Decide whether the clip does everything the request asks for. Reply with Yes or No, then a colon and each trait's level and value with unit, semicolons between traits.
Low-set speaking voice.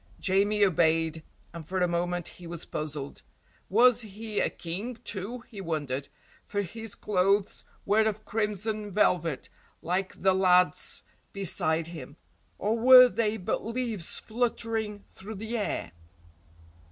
No: high, 200 Hz